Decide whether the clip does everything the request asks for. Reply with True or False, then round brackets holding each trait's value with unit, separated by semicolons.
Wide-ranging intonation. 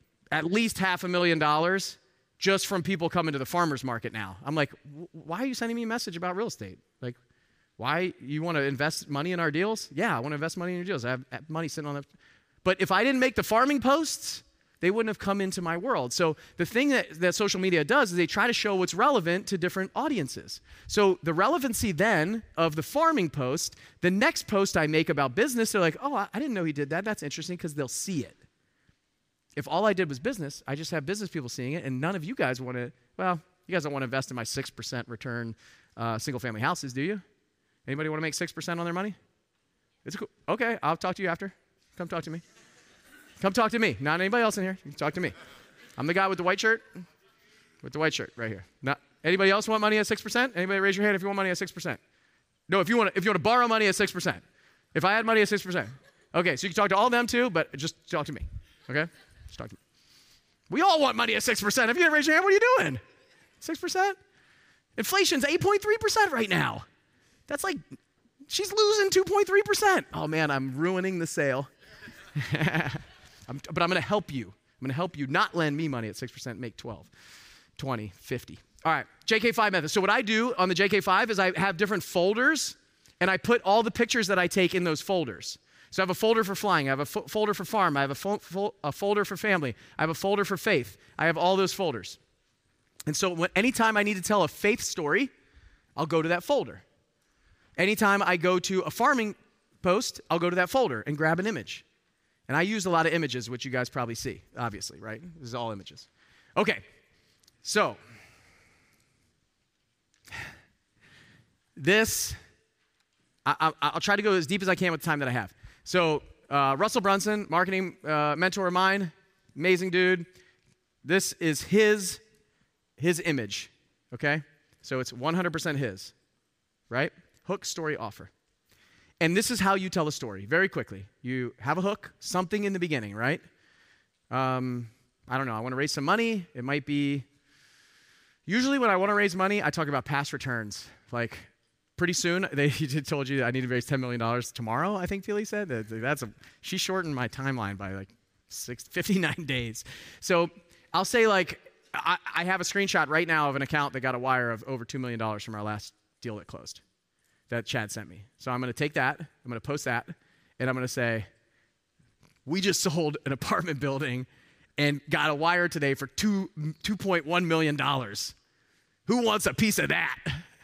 True (6.5 semitones)